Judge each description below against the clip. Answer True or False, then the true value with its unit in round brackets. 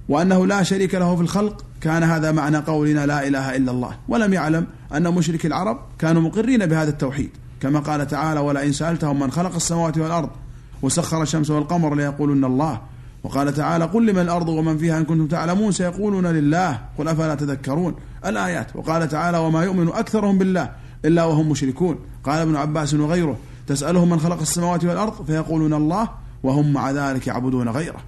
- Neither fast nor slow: False (170 wpm)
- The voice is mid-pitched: True (155 Hz)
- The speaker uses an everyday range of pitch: True (3.5 semitones)